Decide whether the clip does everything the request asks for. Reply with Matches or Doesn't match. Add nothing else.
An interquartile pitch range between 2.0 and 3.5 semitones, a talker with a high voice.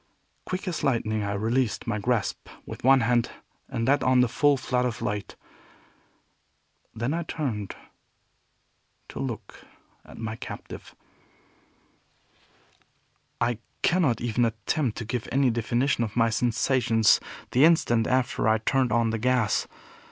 Doesn't match